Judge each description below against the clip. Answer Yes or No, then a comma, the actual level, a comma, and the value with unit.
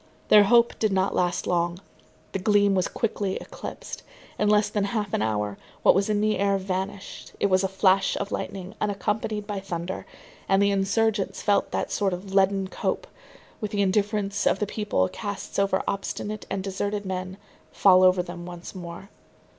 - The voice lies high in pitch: Yes, high, 195 Hz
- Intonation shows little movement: Yes, narrow, 1.8 semitones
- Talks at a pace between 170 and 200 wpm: Yes, average, 180 wpm